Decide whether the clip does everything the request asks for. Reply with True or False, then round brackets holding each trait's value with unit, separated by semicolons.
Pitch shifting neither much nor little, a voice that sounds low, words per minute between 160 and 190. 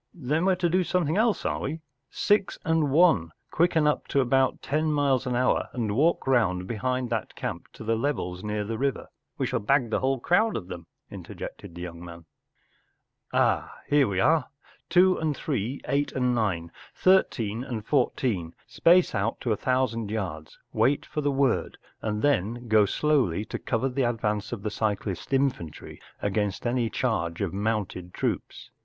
False (5.8 semitones; 120 Hz; 180 wpm)